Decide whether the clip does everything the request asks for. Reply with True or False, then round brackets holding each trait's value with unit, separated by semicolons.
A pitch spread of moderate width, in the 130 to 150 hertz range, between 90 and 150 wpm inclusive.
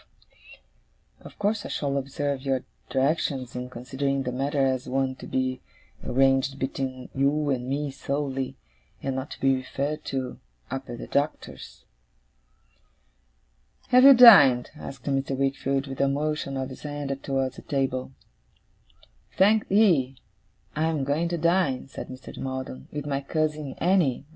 False (2.1 semitones; 135 Hz; 145 wpm)